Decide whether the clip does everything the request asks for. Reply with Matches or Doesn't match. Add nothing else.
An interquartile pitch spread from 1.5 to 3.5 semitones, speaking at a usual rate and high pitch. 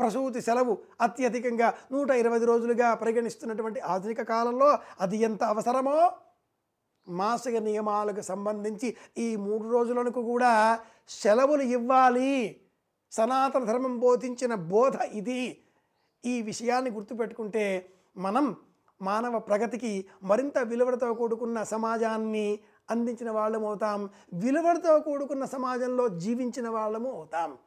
Matches